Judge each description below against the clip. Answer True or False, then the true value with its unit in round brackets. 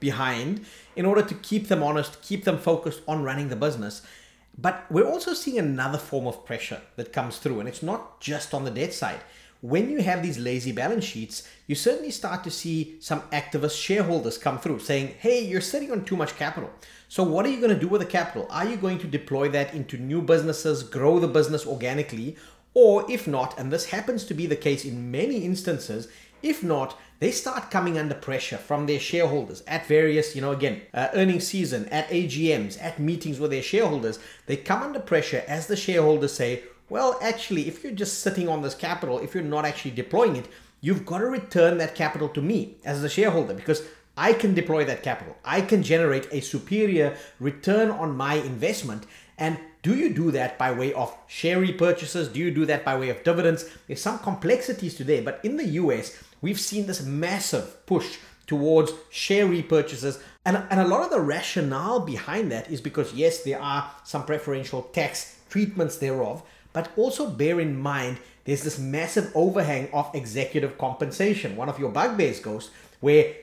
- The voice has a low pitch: False (160 Hz)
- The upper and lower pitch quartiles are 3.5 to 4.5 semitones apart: False (5.0 semitones)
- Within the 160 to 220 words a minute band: True (195 wpm)